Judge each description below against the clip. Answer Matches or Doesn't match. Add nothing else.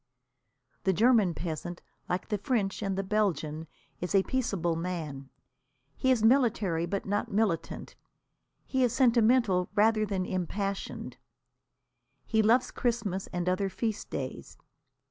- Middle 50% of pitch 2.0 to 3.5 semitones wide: Doesn't match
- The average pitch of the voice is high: Matches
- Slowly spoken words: Matches